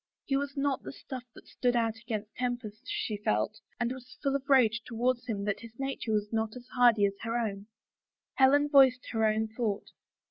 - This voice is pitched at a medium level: No, high, 235 Hz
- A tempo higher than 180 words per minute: Yes, average, 200 wpm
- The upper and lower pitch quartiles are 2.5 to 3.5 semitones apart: Yes, average, 3.1 semitones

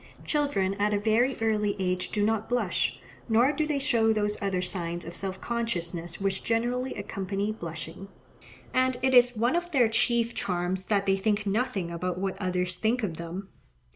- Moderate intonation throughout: Yes, average, 4.4 semitones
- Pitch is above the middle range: Yes, high, 205 Hz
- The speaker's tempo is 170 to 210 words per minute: Yes, average, 175 wpm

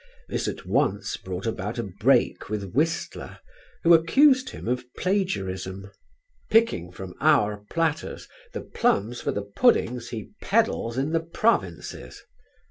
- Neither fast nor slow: No, slow, 130 wpm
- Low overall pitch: Yes, low, 120 Hz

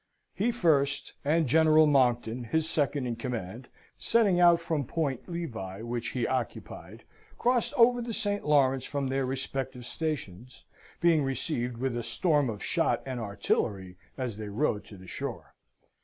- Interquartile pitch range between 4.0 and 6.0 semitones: Yes, average, 5.2 semitones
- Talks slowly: No, average, 155 wpm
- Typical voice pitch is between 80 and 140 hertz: Yes, low, 135 Hz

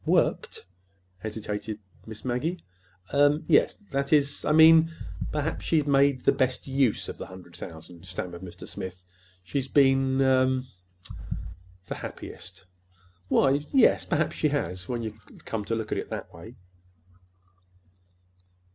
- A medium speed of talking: No, slow, 125 wpm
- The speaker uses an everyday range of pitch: No, wide, 7.3 semitones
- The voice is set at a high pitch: No, low, 130 Hz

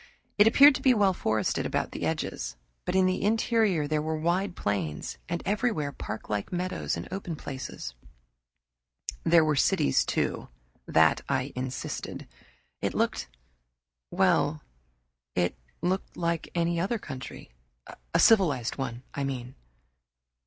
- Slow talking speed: Yes, slow, 130 wpm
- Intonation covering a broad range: Yes, wide, 6.6 semitones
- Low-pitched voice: No, medium, 160 Hz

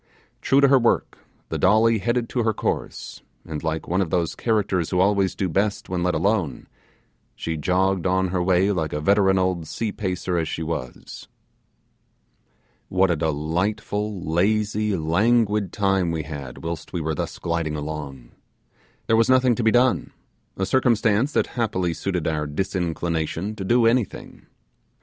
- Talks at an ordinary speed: Yes, average, 160 wpm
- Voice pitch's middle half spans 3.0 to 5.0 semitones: Yes, average, 4.6 semitones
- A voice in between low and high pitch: No, very low, 95 Hz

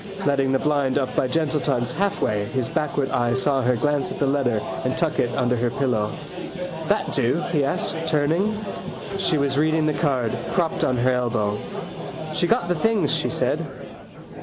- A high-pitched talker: No, medium, 140 Hz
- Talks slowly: No, average, 180 wpm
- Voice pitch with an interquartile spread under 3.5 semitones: No, average, 3.9 semitones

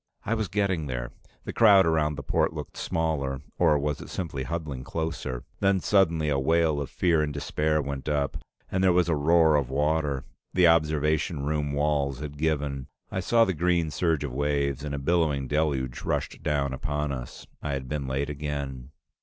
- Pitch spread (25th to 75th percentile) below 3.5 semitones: Yes, average, 2.8 semitones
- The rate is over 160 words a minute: Yes, average, 185 wpm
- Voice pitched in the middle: No, very low, 75 Hz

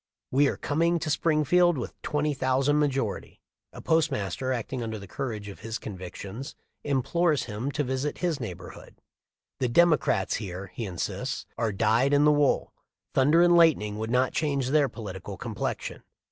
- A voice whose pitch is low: Yes, low, 130 Hz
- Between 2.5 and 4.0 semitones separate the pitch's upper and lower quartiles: No, wide, 5.4 semitones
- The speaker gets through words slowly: No, average, 155 wpm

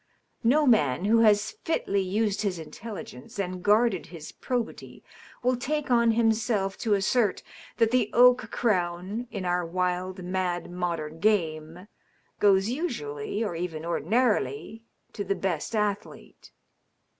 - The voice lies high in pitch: Yes, high, 200 Hz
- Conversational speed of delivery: No, slow, 130 wpm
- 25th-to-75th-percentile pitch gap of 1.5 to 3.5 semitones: No, average, 4.4 semitones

